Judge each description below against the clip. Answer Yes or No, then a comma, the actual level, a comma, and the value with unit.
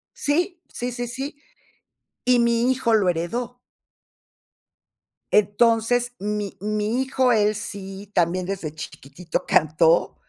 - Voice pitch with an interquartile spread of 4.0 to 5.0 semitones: Yes, average, 4.5 semitones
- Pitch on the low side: No, high, 215 Hz